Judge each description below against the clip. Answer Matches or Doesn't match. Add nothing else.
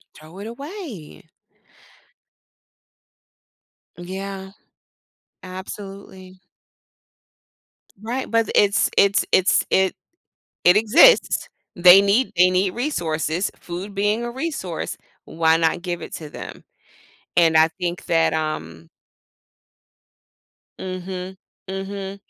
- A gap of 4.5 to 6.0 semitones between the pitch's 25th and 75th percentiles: Doesn't match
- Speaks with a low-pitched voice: Doesn't match